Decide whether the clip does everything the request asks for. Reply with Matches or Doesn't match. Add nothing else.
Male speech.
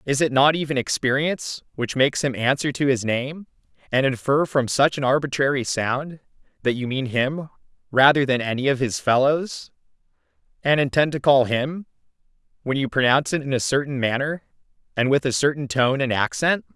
Matches